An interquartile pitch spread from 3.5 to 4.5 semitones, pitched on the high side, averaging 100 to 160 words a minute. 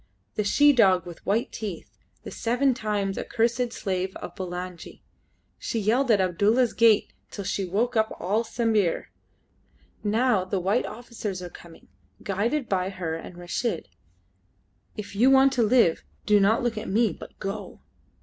Yes: average, 3.9 semitones; high, 210 Hz; average, 155 wpm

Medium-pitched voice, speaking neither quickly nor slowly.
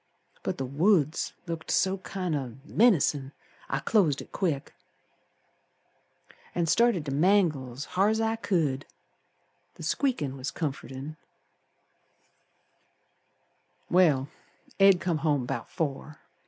No: medium, 155 Hz; slow, 105 wpm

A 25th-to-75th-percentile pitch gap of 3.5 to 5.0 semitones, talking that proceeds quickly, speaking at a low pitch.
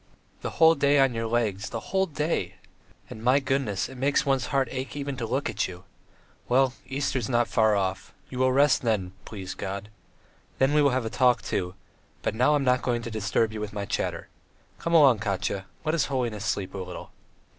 Yes: average, 4.4 semitones; fast, 210 wpm; low, 120 Hz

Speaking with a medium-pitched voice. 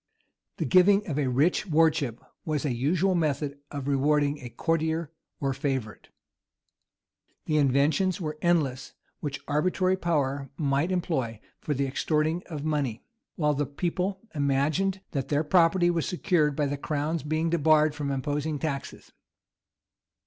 Yes: medium, 150 Hz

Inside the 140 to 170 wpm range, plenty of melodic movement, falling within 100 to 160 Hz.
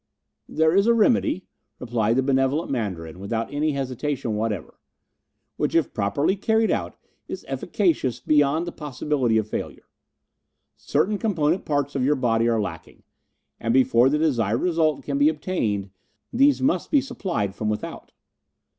Yes: average, 145 wpm; wide, 6.2 semitones; medium, 140 Hz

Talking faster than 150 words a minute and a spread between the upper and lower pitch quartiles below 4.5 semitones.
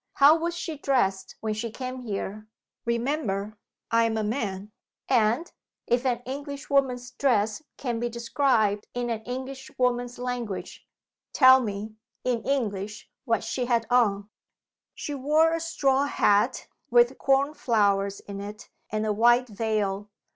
No: average, 140 wpm; average, 3.8 semitones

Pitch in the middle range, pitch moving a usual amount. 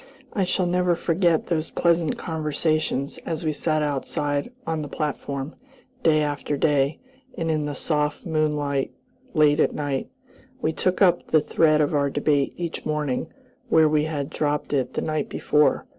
No: medium, 155 Hz; narrow, 1.9 semitones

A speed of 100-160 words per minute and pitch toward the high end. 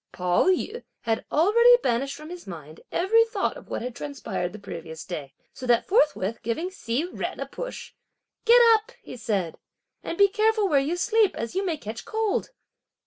No: average, 185 wpm; very high, 300 Hz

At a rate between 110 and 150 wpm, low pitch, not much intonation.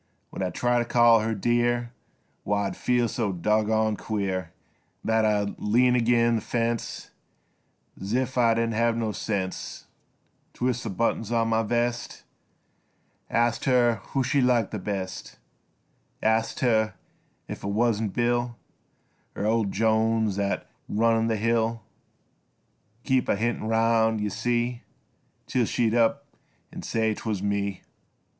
Yes: slow, 135 wpm; low, 115 Hz; narrow, 1.9 semitones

